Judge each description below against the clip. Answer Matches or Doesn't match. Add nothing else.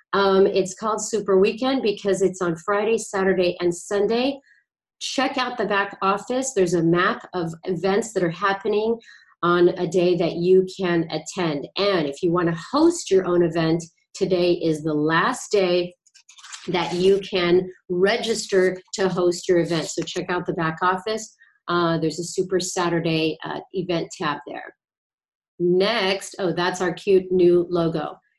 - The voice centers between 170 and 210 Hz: Matches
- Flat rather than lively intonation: Matches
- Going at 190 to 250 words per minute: Doesn't match